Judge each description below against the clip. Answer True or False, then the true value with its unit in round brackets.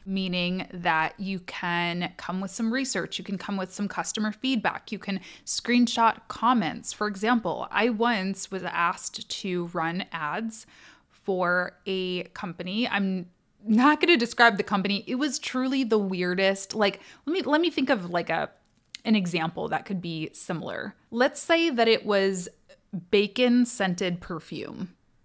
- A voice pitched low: False (200 Hz)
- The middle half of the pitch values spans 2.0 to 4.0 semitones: False (4.6 semitones)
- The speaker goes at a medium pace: True (155 wpm)